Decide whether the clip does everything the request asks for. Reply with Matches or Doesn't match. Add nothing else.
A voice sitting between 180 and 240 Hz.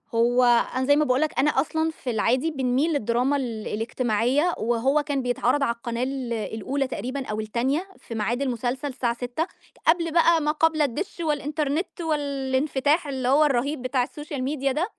Doesn't match